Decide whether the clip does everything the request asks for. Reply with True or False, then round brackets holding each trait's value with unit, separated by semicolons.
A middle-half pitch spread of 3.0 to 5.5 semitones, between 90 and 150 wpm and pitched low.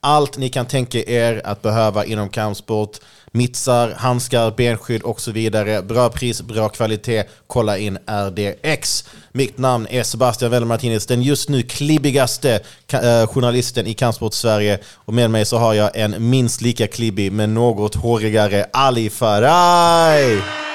False (2.6 semitones; 145 wpm; 115 Hz)